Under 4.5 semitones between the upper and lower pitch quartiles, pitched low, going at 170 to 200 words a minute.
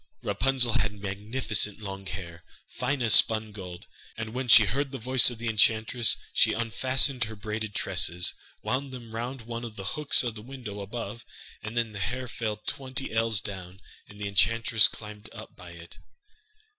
Yes: average, 3.0 semitones; low, 110 Hz; average, 175 wpm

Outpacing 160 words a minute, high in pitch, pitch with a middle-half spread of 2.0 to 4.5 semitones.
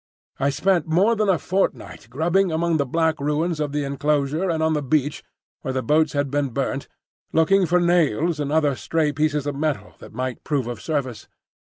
No: average, 195 wpm; medium, 150 Hz; average, 2.8 semitones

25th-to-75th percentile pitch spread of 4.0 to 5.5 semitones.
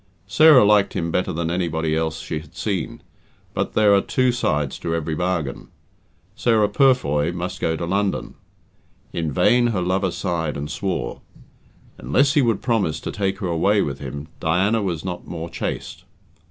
Yes: average, 4.4 semitones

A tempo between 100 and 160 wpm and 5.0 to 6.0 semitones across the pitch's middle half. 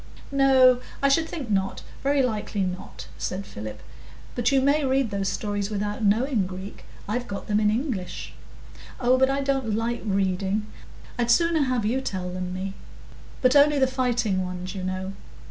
No: average, 170 wpm; average, 5.3 semitones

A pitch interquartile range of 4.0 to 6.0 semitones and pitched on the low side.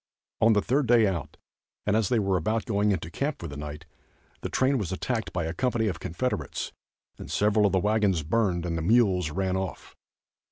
Yes: average, 4.6 semitones; low, 100 Hz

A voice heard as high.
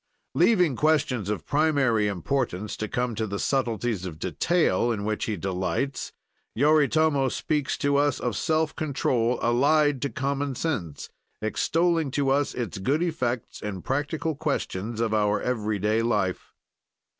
No: low, 125 Hz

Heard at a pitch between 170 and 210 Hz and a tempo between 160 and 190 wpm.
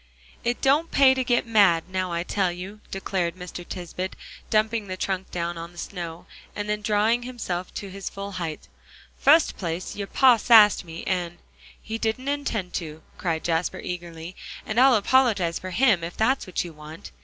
Yes: high, 190 Hz; average, 180 wpm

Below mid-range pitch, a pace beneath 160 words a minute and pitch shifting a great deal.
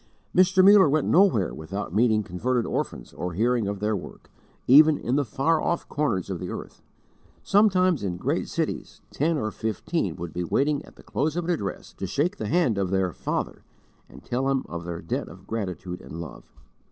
No: low, 115 Hz; average, 195 wpm; wide, 8.9 semitones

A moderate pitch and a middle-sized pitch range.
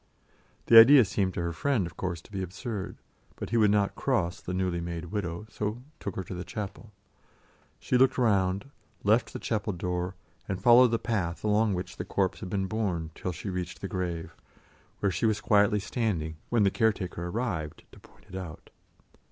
No: very low, 95 Hz; average, 3.6 semitones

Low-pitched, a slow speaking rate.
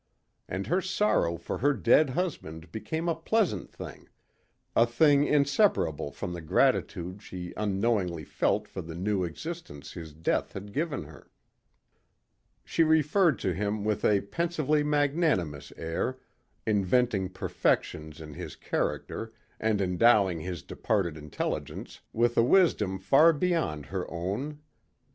Yes: low, 105 Hz; slow, 130 wpm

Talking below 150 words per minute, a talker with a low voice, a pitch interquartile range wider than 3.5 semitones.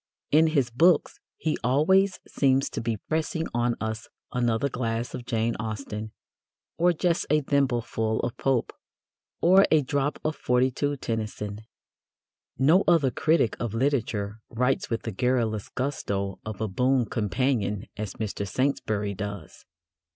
Yes: slow, 135 wpm; low, 125 Hz; average, 4.4 semitones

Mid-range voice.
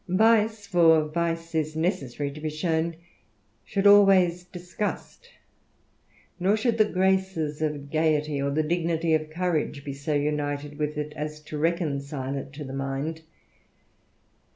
Yes: medium, 155 Hz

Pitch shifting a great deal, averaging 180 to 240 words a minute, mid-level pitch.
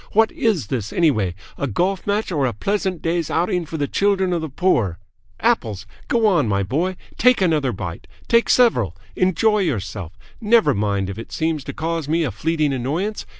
Yes: wide, 8.8 semitones; average, 185 wpm; medium, 160 Hz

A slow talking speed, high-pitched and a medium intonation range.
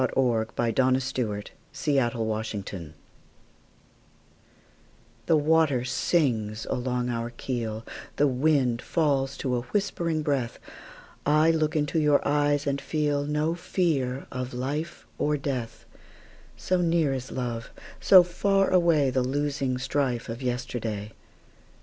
No: slow, 105 wpm; low, 135 Hz; average, 3.8 semitones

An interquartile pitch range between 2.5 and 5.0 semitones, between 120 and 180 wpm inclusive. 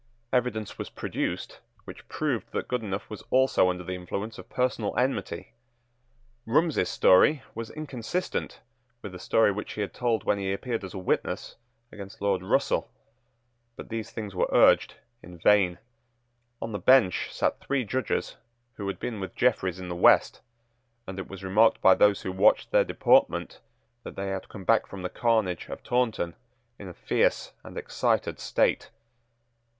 Yes: average, 3.6 semitones; average, 165 wpm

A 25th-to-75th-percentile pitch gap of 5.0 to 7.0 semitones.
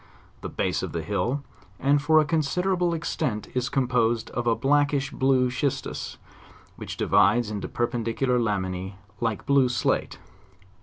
No: average, 4.0 semitones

